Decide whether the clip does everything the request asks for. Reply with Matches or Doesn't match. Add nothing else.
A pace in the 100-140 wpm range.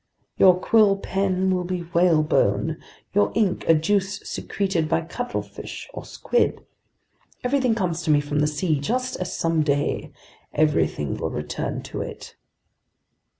Matches